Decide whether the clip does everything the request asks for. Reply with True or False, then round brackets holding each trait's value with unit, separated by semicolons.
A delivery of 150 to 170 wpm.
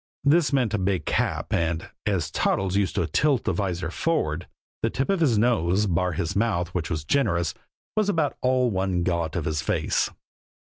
False (185 wpm)